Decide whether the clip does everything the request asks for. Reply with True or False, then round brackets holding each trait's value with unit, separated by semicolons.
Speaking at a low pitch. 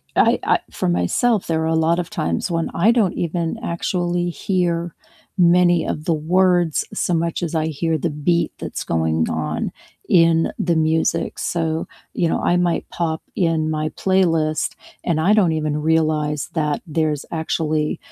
False (165 Hz)